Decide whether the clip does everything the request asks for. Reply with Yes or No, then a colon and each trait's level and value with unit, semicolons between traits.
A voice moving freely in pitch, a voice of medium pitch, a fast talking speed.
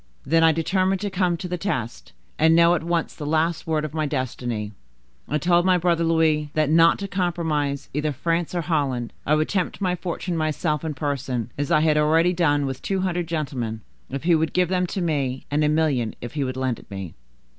No: average, 3.4 semitones; medium, 155 Hz; fast, 215 wpm